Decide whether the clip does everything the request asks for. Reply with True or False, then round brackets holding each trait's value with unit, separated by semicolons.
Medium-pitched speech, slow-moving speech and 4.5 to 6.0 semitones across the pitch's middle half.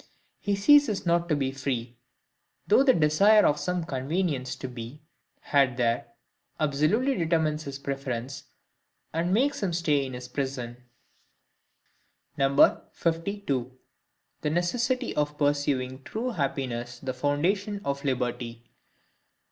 True (145 Hz; 115 wpm; 5.2 semitones)